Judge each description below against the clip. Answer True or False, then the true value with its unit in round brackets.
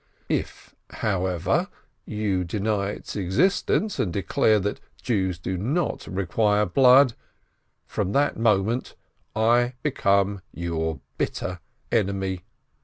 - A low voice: True (100 Hz)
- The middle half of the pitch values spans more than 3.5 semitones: True (3.9 semitones)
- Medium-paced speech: False (105 wpm)